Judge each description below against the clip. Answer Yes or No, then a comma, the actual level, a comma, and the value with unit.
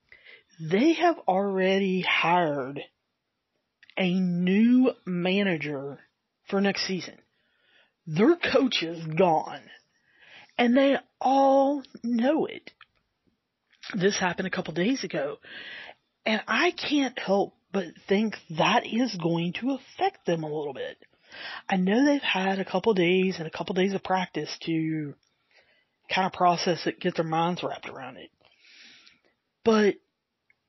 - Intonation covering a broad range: Yes, wide, 6.4 semitones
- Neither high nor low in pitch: No, high, 195 Hz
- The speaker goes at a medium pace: No, slow, 130 wpm